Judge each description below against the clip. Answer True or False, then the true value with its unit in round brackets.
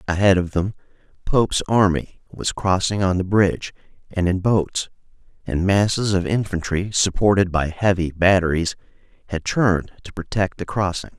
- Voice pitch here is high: False (95 Hz)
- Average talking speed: True (145 wpm)